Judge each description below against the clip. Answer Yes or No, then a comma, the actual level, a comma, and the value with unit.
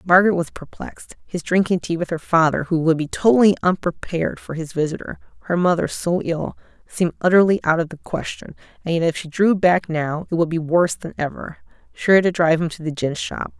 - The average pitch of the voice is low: No, medium, 170 Hz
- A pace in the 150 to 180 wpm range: No, average, 200 wpm